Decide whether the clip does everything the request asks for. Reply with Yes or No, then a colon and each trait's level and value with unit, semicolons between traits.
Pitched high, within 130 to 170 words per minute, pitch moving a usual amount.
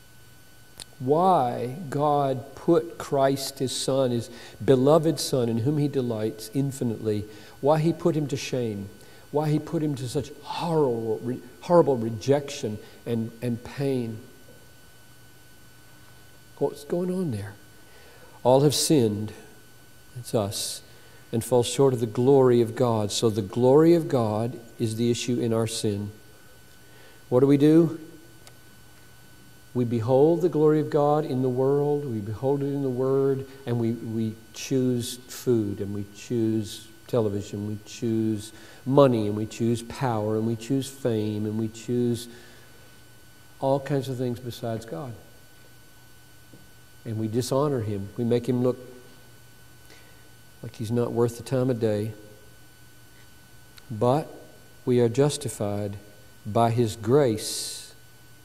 No: low, 120 Hz; slow, 135 wpm; average, 3.9 semitones